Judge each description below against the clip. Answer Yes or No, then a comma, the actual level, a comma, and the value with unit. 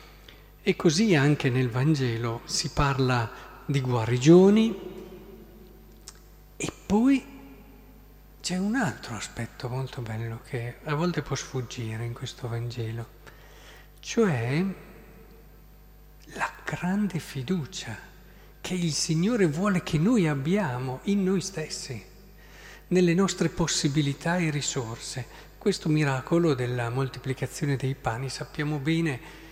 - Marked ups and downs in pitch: Yes, wide, 6.1 semitones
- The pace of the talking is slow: Yes, slow, 105 wpm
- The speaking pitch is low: No, medium, 150 Hz